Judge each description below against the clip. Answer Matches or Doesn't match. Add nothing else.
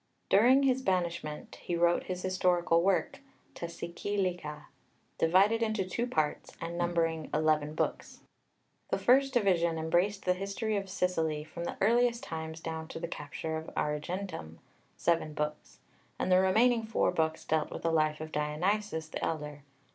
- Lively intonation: Doesn't match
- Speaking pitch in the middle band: Matches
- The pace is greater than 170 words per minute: Doesn't match